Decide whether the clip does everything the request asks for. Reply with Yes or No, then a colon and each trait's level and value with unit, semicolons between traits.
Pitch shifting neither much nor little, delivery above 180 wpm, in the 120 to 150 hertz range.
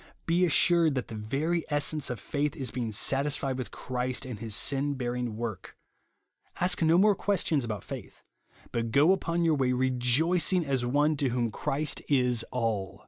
No: average, 4.4 semitones; average, 170 wpm; low, 135 Hz